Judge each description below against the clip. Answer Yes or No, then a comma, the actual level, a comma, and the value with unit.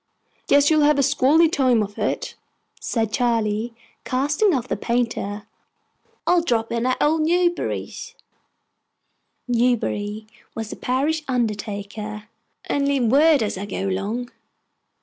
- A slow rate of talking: Yes, slow, 130 wpm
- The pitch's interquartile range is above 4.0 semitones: Yes, average, 4.9 semitones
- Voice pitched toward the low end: No, high, 245 Hz